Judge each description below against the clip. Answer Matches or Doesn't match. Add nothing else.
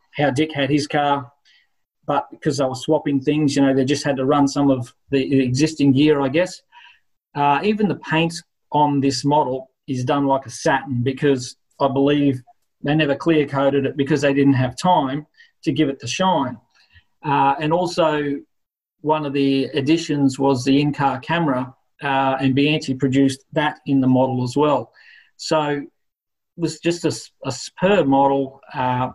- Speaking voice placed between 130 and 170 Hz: Matches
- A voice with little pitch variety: Matches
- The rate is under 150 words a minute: Doesn't match